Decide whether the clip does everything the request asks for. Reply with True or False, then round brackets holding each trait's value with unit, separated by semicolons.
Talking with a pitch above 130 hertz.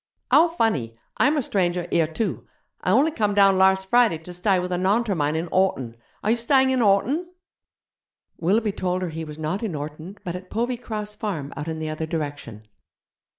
True (190 Hz)